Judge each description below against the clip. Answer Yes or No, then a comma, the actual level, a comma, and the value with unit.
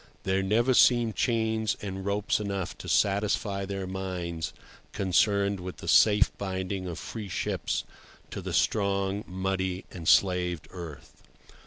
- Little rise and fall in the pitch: Yes, narrow, 1.9 semitones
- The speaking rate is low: Yes, slow, 130 wpm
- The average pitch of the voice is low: Yes, very low, 95 Hz